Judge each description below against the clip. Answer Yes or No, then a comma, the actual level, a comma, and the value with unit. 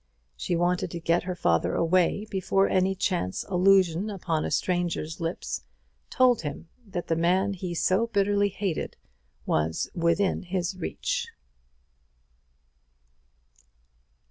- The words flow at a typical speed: No, slow, 115 wpm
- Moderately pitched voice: Yes, medium, 180 Hz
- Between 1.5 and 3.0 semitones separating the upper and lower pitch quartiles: Yes, narrow, 2.5 semitones